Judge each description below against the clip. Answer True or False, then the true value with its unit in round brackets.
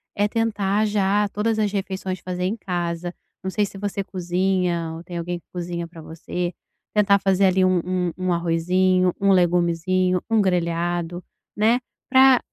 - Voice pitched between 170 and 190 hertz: True (185 Hz)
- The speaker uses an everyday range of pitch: False (2.3 semitones)